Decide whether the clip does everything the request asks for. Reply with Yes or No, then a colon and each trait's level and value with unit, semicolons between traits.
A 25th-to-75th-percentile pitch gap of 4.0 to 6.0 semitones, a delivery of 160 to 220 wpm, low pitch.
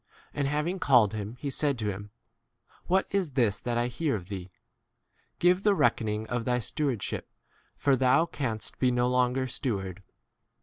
Yes: average, 4.8 semitones; average, 175 wpm; low, 125 Hz